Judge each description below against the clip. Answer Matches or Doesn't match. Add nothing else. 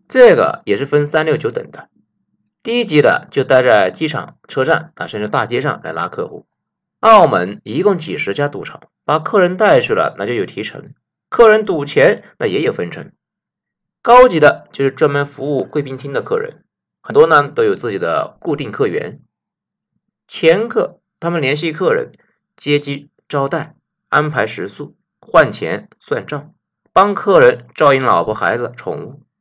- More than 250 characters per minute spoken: Doesn't match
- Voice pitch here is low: Doesn't match